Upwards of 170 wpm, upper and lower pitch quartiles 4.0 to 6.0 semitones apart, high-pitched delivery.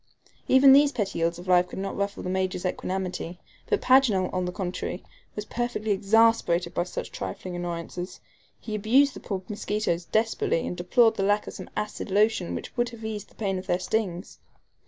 No: average, 190 wpm; average, 3.6 semitones; high, 195 Hz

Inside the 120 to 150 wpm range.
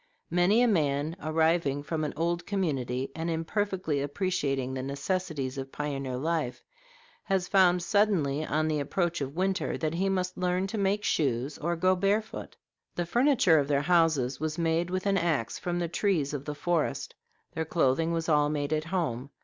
No: average, 175 wpm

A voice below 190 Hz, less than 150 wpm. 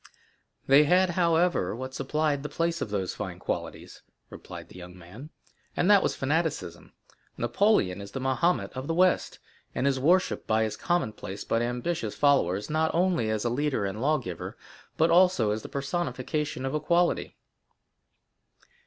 No: medium, 140 Hz; average, 155 wpm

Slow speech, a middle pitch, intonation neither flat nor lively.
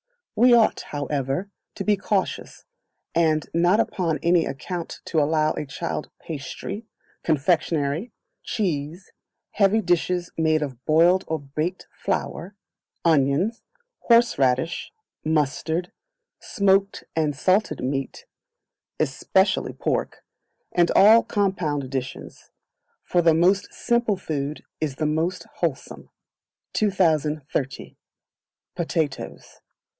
Yes: slow, 100 wpm; medium, 165 Hz; average, 4.4 semitones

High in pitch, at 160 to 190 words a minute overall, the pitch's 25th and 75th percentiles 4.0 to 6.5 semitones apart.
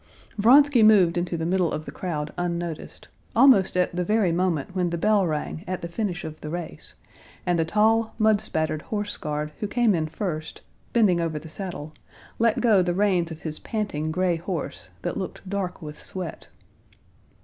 No: medium, 180 Hz; average, 180 wpm; average, 4.3 semitones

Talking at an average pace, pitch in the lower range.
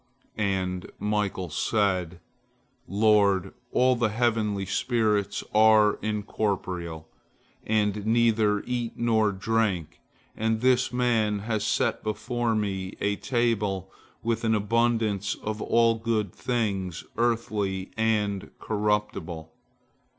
No: slow, 100 wpm; low, 105 Hz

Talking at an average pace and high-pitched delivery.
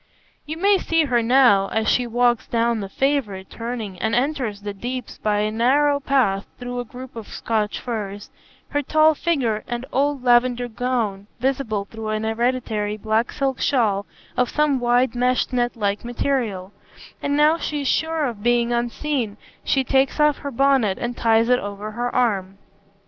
Yes: average, 170 wpm; high, 240 Hz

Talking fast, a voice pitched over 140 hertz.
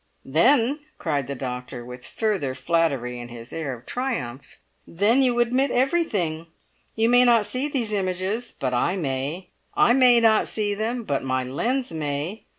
No: average, 160 wpm; medium, 185 Hz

